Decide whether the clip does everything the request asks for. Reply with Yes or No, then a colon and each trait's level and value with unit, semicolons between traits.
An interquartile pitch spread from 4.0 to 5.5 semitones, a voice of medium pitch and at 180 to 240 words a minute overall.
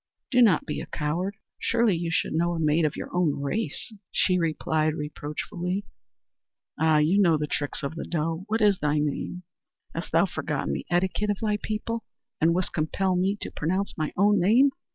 Yes: average, 4.6 semitones; medium, 175 Hz; average, 190 wpm